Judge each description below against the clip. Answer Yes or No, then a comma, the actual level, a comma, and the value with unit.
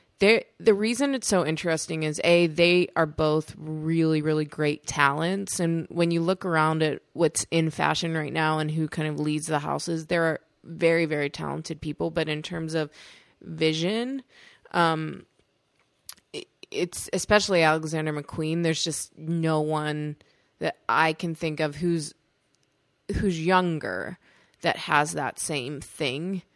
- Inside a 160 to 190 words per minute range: No, average, 150 wpm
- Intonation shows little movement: Yes, narrow, 1.8 semitones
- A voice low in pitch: No, medium, 160 Hz